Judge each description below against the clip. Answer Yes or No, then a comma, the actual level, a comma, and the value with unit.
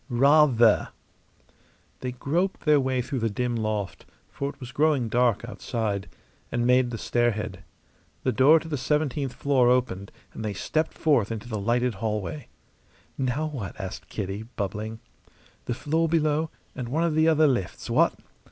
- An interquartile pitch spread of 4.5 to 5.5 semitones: Yes, average, 4.9 semitones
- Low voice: Yes, low, 125 Hz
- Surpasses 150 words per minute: Yes, average, 160 wpm